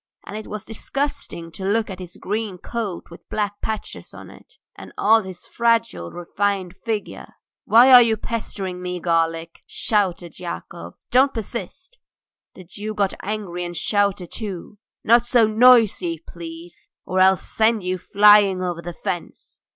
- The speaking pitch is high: Yes, high, 200 Hz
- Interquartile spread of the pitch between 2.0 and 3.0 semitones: No, average, 3.9 semitones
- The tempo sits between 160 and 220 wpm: No, average, 150 wpm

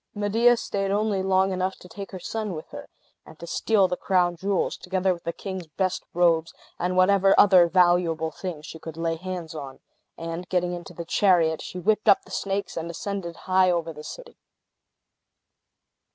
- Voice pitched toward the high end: No, medium, 180 Hz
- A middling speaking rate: Yes, average, 180 wpm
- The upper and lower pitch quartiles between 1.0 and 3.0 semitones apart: Yes, narrow, 2.5 semitones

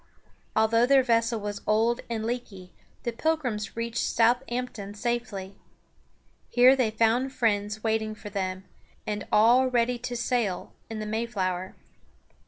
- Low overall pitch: No, high, 225 Hz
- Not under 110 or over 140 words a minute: Yes, slow, 135 wpm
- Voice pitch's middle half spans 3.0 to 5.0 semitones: No, narrow, 2.6 semitones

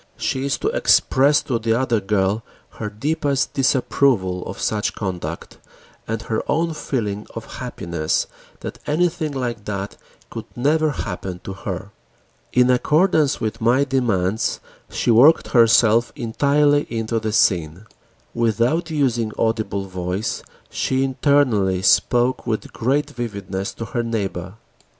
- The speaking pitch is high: No, low, 115 Hz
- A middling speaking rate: No, slow, 130 wpm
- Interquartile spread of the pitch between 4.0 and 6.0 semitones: Yes, average, 5.2 semitones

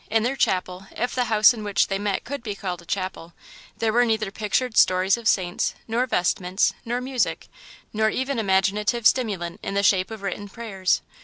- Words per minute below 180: No, average, 190 wpm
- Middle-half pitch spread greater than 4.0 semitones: No, average, 3.5 semitones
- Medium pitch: No, high, 210 Hz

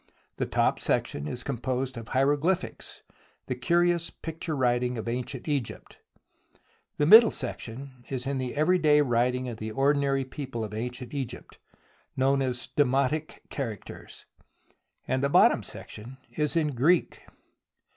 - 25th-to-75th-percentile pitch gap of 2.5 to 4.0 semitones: Yes, average, 3.1 semitones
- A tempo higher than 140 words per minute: No, slow, 135 wpm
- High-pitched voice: No, low, 135 Hz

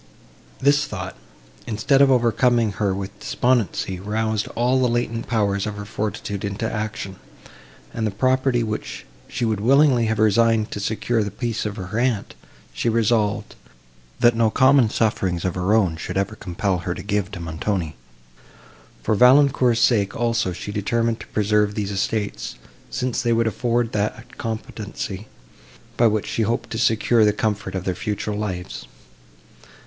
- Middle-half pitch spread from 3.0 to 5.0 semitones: No, narrow, 2.6 semitones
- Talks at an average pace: Yes, average, 160 wpm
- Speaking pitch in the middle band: No, low, 110 Hz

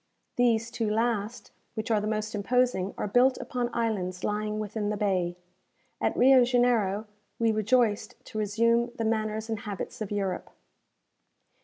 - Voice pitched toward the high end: Yes, high, 220 Hz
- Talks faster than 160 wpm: No, average, 150 wpm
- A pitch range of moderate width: No, narrow, 2.3 semitones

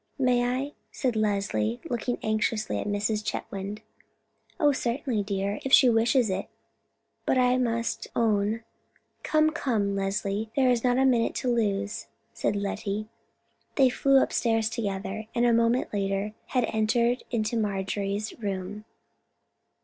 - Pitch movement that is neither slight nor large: Yes, average, 3.3 semitones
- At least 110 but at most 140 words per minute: Yes, slow, 135 wpm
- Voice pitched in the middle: No, high, 220 Hz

